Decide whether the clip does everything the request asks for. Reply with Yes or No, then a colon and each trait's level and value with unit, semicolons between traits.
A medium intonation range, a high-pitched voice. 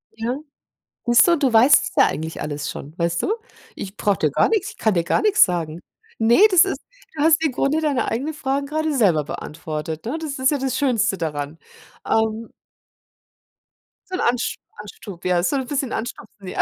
No: wide, 8.7 semitones; high, 230 Hz